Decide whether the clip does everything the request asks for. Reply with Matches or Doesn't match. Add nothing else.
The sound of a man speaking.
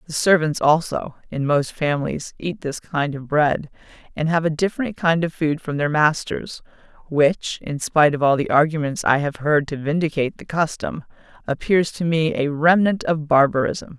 Doesn't match